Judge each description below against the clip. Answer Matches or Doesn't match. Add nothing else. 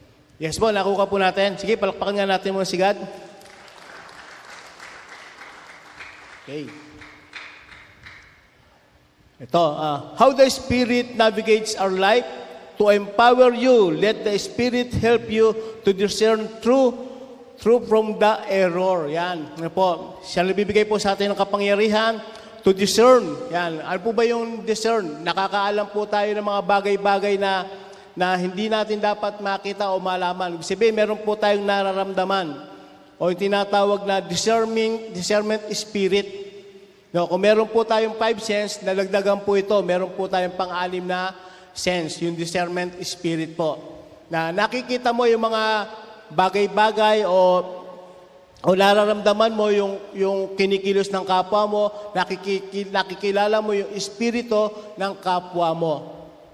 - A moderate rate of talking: Matches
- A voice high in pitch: Matches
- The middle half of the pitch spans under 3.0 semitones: Matches